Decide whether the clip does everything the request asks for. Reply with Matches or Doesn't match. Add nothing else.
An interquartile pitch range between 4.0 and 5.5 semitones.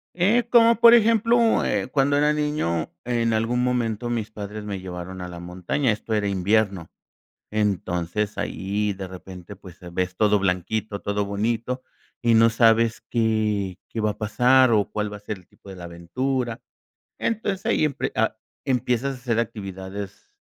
Matches